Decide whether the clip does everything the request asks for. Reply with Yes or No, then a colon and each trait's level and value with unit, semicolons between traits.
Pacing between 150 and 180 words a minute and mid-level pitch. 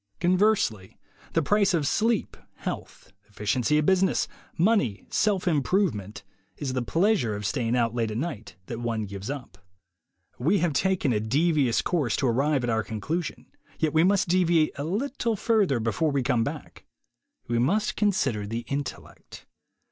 Yes: average, 155 wpm; medium, 145 Hz